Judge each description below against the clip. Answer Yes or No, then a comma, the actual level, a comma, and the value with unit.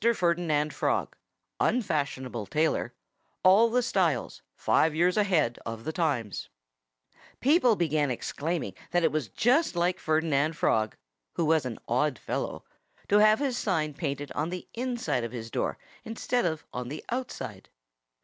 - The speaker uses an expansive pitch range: Yes, wide, 6.0 semitones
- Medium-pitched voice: Yes, medium, 160 Hz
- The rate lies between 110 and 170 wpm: Yes, average, 145 wpm